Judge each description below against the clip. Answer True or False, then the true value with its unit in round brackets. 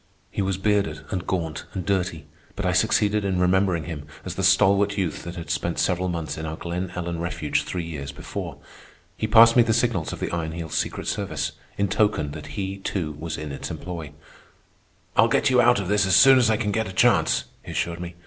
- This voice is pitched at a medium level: False (90 Hz)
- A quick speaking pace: True (220 wpm)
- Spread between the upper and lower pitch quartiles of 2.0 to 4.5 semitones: True (3.5 semitones)